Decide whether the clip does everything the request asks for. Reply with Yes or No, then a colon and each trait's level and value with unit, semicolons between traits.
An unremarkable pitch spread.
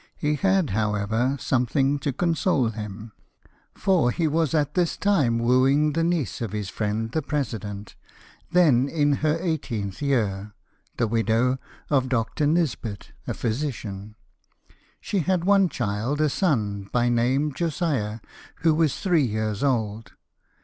No: wide, 5.9 semitones